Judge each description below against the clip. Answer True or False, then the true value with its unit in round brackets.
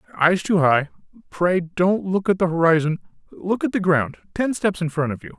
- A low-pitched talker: False (175 Hz)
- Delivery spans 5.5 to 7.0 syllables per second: False (5.0 syllables/s)